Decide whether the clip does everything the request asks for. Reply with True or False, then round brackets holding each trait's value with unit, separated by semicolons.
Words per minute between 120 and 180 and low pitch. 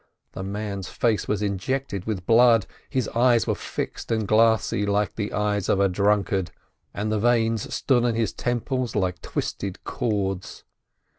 True (155 wpm; 105 Hz)